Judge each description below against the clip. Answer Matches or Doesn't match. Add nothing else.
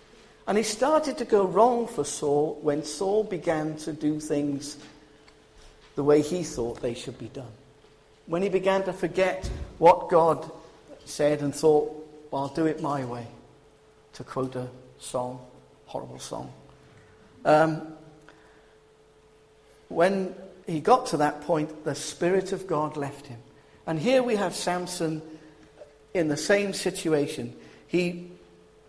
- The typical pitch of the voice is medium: Matches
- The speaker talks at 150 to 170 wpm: Doesn't match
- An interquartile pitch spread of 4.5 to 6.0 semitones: Doesn't match